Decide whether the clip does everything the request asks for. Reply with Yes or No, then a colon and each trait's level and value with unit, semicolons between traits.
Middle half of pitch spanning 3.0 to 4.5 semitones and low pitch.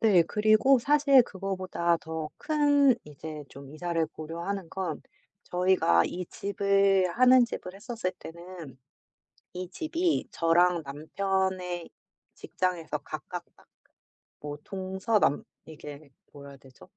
No: average, 3.9 semitones; medium, 185 Hz